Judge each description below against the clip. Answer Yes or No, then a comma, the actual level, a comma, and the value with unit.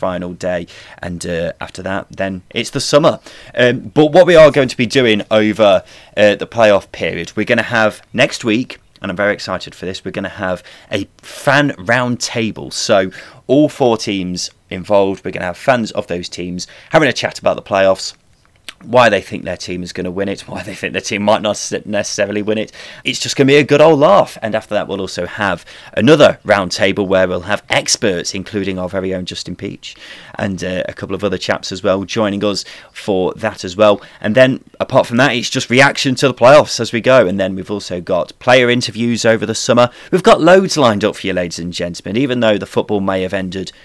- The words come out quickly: Yes, fast, 225 wpm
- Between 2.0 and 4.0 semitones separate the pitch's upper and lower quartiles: No, average, 4.5 semitones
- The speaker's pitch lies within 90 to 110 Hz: Yes, low, 105 Hz